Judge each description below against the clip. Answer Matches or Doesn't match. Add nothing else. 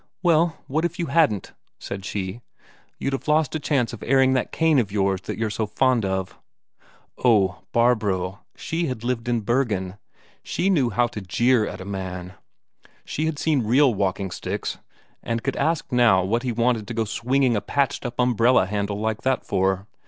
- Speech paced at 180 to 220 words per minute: Matches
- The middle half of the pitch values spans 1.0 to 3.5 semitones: Doesn't match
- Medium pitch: Doesn't match